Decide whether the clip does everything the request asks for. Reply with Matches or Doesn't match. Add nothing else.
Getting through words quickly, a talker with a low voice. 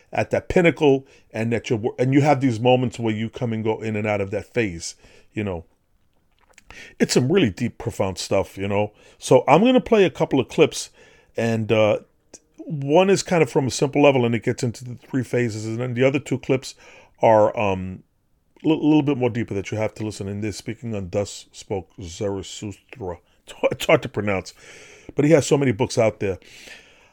Matches